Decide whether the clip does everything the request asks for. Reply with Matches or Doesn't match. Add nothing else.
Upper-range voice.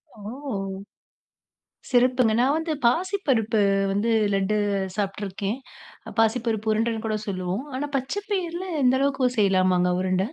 Matches